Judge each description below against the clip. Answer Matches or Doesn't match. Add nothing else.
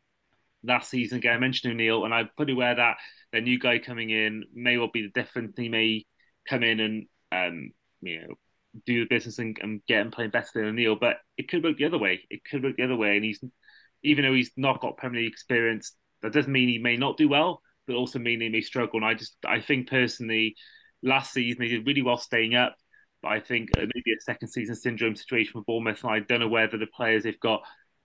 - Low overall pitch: Matches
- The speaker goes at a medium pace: Doesn't match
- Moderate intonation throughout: Doesn't match